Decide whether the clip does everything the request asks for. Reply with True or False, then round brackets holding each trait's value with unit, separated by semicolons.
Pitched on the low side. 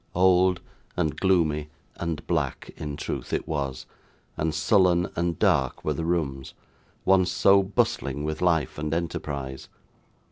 True (80 Hz)